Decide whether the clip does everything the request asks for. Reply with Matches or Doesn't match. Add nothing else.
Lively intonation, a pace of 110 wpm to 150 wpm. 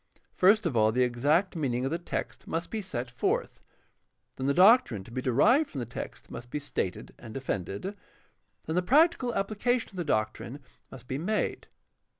Doesn't match